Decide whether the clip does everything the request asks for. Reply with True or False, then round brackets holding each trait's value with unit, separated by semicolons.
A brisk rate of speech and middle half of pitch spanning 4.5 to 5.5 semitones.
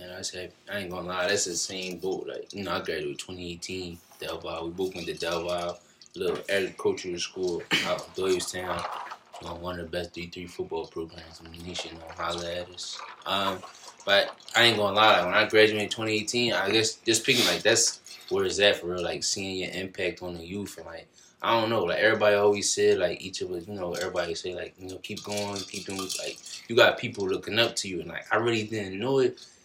True (235 wpm; 4.9 semitones)